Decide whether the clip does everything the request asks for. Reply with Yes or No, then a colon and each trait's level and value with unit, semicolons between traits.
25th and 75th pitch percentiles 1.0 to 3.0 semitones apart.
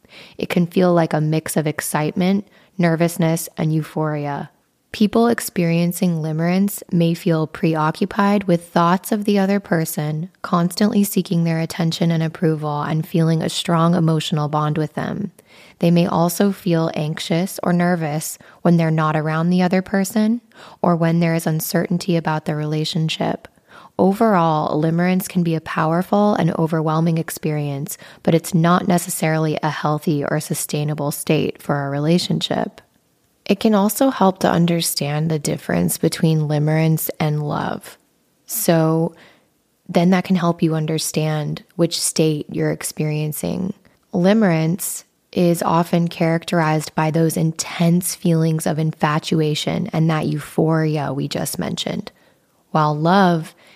Yes: narrow, 2.5 semitones